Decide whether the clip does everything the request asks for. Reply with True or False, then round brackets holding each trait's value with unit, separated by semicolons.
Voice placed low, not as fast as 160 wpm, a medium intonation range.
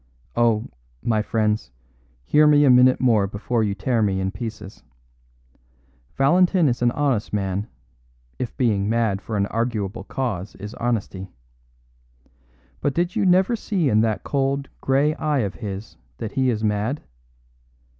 True (115 Hz; 145 wpm; 4.7 semitones)